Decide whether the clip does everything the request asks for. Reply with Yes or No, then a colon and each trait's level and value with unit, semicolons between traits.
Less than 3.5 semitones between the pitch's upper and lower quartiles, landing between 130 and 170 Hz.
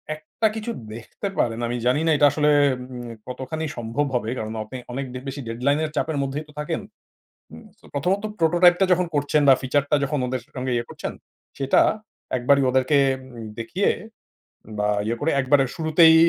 No: average, 3.8 semitones; medium, 140 Hz